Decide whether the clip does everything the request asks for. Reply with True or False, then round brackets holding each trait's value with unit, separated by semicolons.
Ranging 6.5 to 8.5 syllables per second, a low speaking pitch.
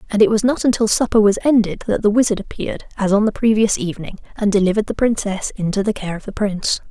False (6.6 syllables/s; 210 Hz)